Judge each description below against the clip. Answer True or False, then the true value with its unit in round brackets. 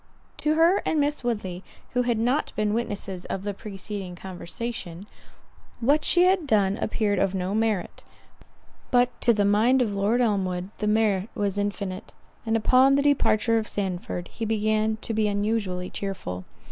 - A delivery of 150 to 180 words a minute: True (160 wpm)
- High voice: True (210 Hz)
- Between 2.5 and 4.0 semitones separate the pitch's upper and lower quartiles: True (3.5 semitones)